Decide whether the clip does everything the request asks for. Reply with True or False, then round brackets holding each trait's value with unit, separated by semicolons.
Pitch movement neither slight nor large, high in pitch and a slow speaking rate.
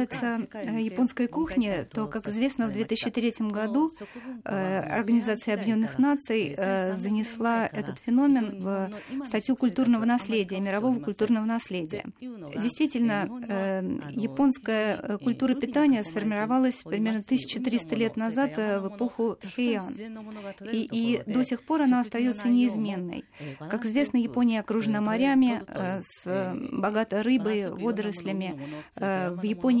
True (3.0 semitones; 225 Hz; 105 wpm)